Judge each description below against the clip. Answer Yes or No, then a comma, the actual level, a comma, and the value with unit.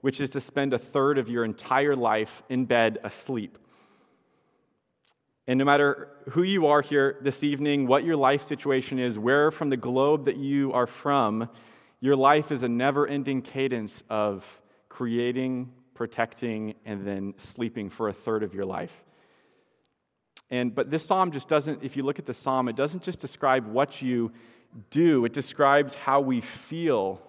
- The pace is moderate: Yes, average, 170 wpm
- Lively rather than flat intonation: No, average, 3.2 semitones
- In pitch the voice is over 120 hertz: Yes, low, 135 Hz